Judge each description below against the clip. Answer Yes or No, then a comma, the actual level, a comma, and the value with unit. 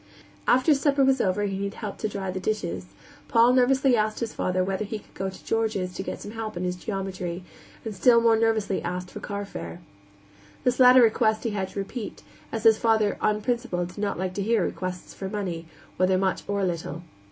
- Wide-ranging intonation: No, average, 3.4 semitones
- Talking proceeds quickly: Yes, fast, 210 wpm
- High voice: Yes, high, 205 Hz